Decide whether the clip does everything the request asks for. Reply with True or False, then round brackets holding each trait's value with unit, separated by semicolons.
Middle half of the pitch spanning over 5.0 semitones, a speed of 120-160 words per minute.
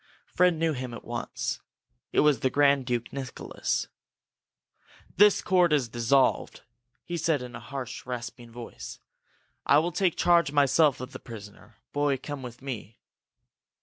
False (4.0 semitones; 150 wpm)